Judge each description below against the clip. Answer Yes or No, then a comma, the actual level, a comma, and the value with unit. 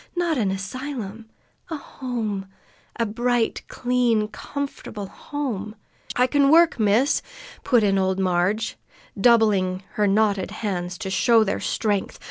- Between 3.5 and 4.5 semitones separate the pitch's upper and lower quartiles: Yes, average, 4.2 semitones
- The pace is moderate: No, slow, 130 wpm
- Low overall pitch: No, high, 220 Hz